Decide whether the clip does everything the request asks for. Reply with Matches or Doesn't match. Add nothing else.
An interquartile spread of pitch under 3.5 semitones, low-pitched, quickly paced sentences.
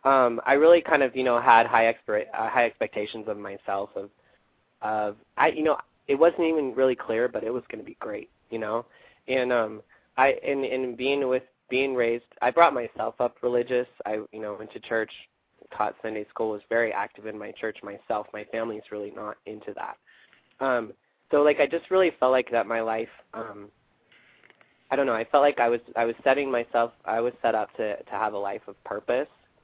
Matches